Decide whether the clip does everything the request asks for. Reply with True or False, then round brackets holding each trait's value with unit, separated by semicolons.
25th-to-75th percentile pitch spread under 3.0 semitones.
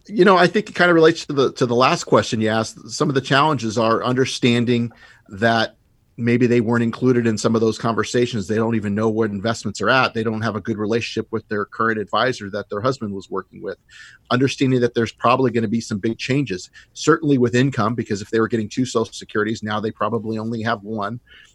True (2.4 semitones)